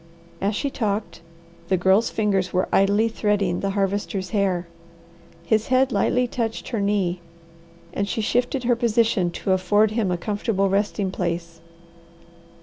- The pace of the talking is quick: No, average, 145 wpm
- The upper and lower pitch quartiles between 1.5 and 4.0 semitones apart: Yes, average, 3.0 semitones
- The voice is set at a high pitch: Yes, high, 200 Hz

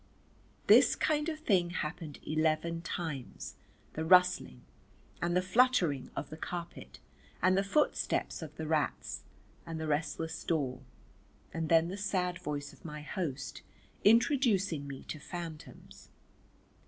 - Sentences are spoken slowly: Yes, slow, 130 wpm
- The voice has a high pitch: No, medium, 165 Hz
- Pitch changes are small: No, average, 3.3 semitones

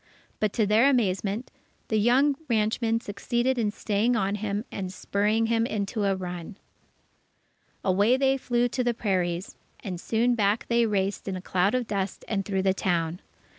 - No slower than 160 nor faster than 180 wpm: Yes, average, 170 wpm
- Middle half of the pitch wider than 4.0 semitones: No, average, 3.4 semitones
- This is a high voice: Yes, high, 210 Hz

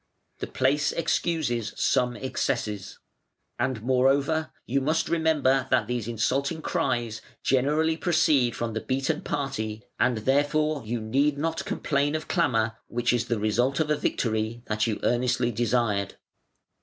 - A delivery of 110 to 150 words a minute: Yes, average, 140 wpm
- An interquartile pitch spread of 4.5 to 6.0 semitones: No, average, 4.1 semitones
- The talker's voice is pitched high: No, low, 130 Hz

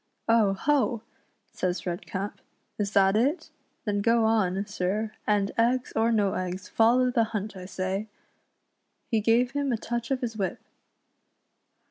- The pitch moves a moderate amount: Yes, average, 3.2 semitones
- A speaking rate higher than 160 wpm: No, average, 150 wpm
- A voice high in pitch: Yes, high, 215 Hz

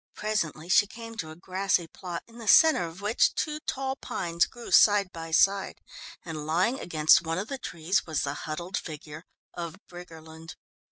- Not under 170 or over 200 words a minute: Yes, average, 175 wpm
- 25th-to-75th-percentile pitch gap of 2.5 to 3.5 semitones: No, average, 4.3 semitones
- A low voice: No, medium, 175 Hz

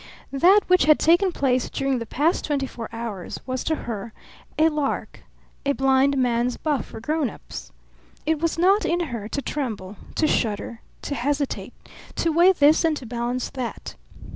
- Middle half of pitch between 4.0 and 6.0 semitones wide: Yes, average, 4.8 semitones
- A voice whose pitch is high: Yes, very high, 275 Hz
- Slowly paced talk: No, average, 165 wpm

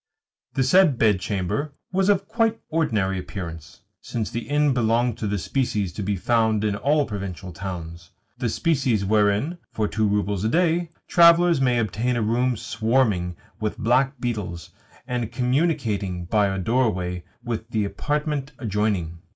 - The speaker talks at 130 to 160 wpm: Yes, average, 150 wpm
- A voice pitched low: Yes, low, 110 Hz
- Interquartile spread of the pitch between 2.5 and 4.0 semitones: No, average, 5.2 semitones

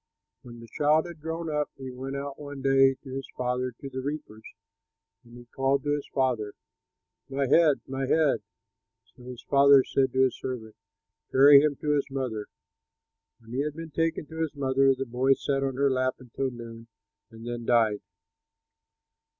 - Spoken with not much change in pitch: Yes, narrow, 2.3 semitones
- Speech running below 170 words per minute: No, average, 180 wpm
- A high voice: No, low, 135 Hz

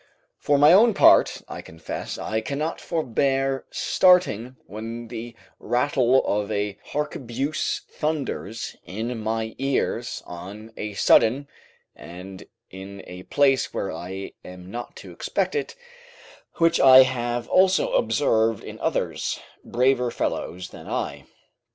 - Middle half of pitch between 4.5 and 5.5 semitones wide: Yes, average, 5.0 semitones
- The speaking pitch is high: No, low, 120 Hz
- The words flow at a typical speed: No, slow, 125 wpm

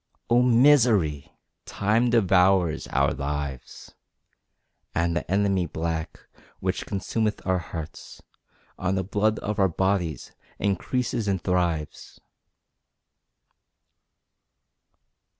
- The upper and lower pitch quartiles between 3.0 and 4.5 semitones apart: Yes, average, 4.1 semitones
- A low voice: Yes, very low, 95 Hz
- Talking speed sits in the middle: No, slow, 90 wpm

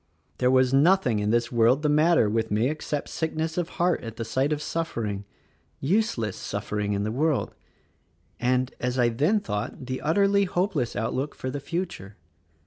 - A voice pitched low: Yes, low, 130 Hz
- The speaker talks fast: No, average, 170 wpm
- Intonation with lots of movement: Yes, wide, 6.0 semitones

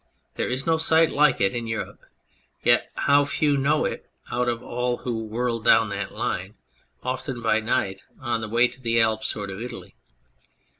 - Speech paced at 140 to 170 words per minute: No, average, 185 wpm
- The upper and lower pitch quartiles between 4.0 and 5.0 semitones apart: No, average, 2.8 semitones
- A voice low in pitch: Yes, low, 120 Hz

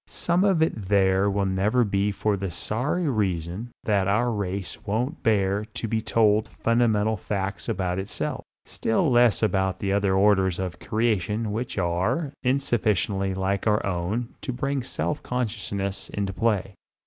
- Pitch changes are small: No, average, 3.2 semitones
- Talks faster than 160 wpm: No, average, 150 wpm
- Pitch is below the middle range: Yes, low, 105 Hz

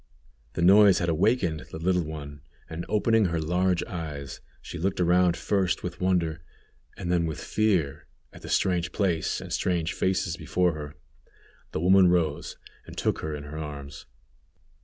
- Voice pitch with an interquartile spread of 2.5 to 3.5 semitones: Yes, average, 2.8 semitones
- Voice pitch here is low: Yes, very low, 85 Hz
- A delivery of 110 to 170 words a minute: Yes, average, 160 wpm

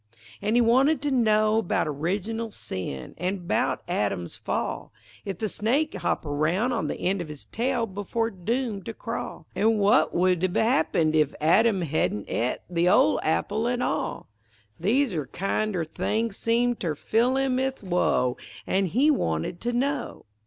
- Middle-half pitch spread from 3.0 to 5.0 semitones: No, wide, 5.5 semitones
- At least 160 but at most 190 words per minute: Yes, average, 165 wpm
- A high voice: Yes, high, 205 Hz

